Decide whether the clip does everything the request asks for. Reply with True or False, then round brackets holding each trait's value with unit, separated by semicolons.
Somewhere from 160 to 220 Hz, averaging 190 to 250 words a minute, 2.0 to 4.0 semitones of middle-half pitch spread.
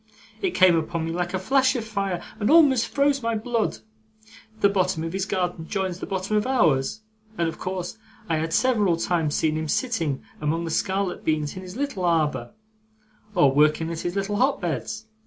False (185 Hz; 195 wpm; 4.9 semitones)